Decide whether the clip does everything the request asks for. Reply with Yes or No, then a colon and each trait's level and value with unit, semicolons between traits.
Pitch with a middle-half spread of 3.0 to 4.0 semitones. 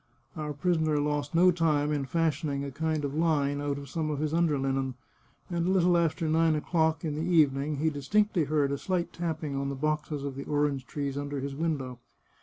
No: narrow, 2.5 semitones